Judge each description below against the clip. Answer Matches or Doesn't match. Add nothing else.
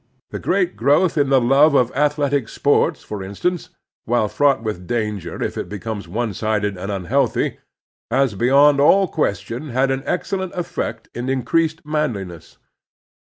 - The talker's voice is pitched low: Matches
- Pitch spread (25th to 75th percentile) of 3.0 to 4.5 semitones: Doesn't match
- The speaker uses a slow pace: Doesn't match